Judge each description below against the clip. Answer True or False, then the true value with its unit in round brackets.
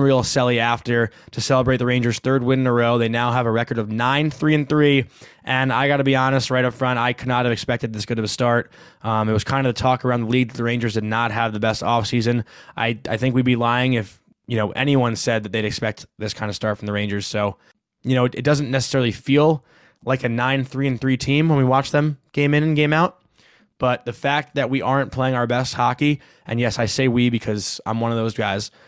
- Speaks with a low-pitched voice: True (125 Hz)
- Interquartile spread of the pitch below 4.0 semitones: True (2.6 semitones)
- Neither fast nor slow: False (260 wpm)